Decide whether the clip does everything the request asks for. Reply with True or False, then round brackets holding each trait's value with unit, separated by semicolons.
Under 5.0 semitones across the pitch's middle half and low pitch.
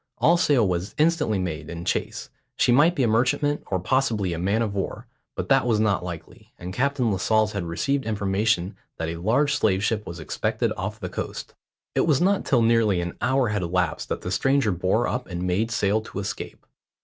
False (5.5 semitones; 105 Hz)